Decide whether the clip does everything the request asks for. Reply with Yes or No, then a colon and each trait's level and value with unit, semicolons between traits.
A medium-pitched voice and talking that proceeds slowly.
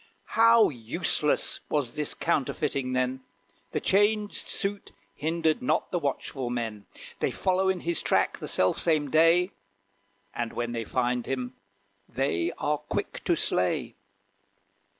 Yes: medium, 145 Hz; slow, 130 wpm